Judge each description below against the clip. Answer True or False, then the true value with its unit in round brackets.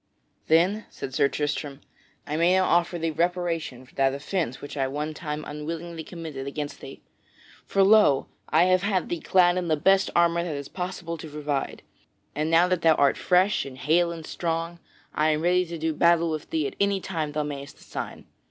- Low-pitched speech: False (165 Hz)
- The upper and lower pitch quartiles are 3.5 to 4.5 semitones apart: False (2.9 semitones)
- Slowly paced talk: False (200 wpm)